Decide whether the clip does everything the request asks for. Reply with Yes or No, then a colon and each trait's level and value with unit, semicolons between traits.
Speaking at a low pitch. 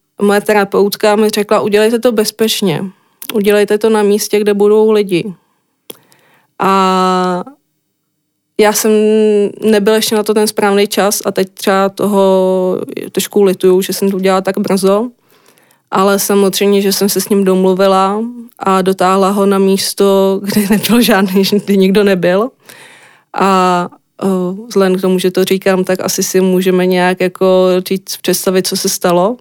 No: high, 195 Hz